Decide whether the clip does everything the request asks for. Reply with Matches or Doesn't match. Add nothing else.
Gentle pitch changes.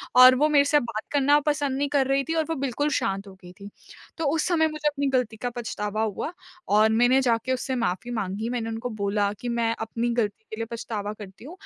Doesn't match